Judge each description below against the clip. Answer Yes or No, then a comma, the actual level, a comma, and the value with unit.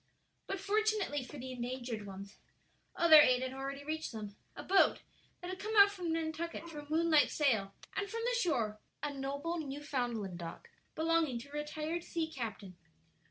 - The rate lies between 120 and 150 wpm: No, average, 170 wpm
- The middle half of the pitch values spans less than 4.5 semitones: No, average, 5.2 semitones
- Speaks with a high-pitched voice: Yes, very high, 295 Hz